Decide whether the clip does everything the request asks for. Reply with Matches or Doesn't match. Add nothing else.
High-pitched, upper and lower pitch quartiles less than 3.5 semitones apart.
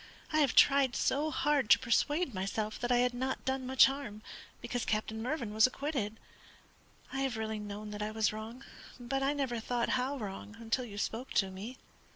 Doesn't match